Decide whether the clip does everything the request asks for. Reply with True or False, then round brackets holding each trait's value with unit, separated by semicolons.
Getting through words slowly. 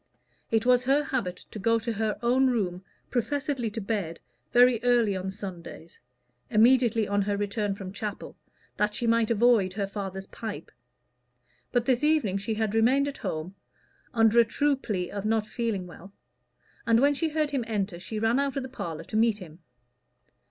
False (180 wpm)